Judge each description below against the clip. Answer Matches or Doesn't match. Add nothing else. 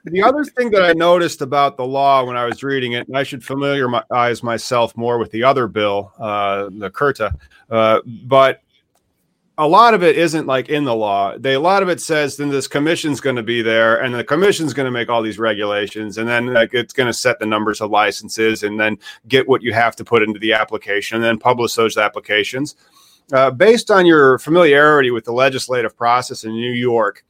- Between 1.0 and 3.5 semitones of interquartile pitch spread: Doesn't match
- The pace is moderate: Doesn't match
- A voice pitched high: Doesn't match